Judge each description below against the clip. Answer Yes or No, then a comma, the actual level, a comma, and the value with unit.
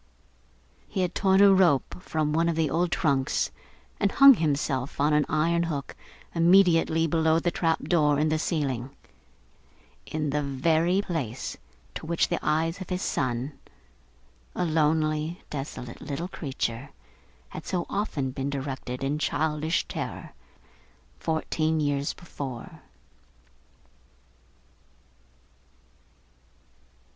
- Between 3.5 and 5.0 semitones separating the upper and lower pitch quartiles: No, average, 3.1 semitones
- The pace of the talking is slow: Yes, slow, 115 wpm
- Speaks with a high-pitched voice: No, medium, 155 Hz